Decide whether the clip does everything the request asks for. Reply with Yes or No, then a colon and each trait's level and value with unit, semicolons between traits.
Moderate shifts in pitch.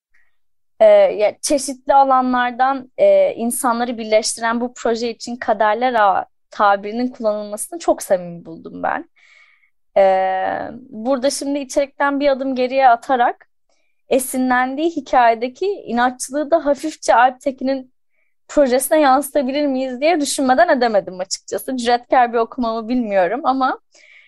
Yes: average, 3.5 semitones